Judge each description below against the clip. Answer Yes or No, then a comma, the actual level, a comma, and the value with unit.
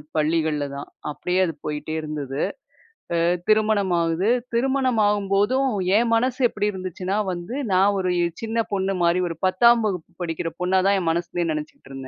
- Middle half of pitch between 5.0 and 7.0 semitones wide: No, average, 4.5 semitones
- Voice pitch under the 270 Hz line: Yes, medium, 185 Hz